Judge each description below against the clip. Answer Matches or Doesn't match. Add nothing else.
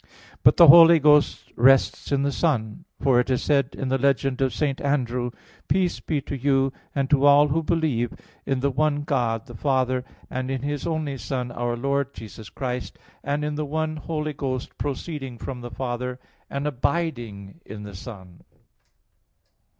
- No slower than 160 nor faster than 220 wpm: Matches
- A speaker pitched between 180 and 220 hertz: Doesn't match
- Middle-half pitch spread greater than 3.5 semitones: Doesn't match